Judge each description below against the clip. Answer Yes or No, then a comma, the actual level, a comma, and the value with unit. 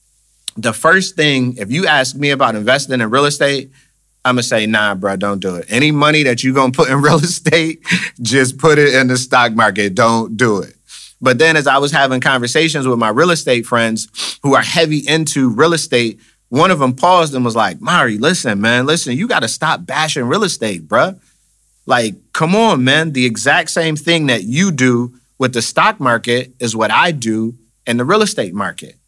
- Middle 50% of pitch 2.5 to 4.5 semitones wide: No, average, 4.9 semitones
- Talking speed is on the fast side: Yes, fast, 210 wpm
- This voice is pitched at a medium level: No, low, 130 Hz